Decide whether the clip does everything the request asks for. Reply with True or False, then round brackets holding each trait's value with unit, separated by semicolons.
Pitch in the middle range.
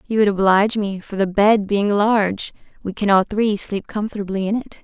False (200 Hz)